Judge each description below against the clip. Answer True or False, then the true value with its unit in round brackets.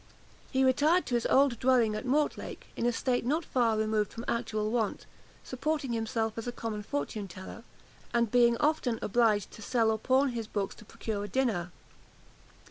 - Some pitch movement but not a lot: True (3.1 semitones)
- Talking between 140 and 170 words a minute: False (180 wpm)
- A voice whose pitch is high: True (235 Hz)